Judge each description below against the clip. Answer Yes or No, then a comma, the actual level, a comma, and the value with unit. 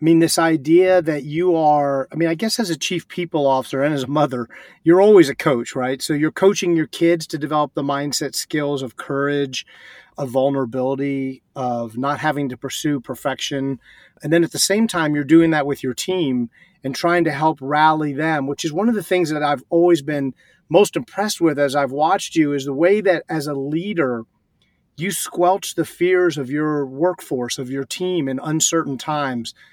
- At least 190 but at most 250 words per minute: Yes, average, 200 wpm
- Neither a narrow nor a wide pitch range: Yes, average, 3.5 semitones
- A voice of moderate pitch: Yes, medium, 155 Hz